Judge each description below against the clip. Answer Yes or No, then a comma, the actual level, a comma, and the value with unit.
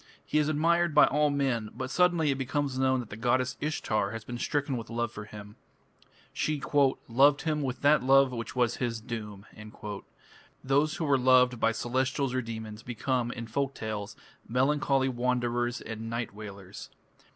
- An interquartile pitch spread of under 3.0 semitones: No, average, 3.5 semitones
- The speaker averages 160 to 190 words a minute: Yes, average, 170 wpm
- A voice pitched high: No, low, 125 Hz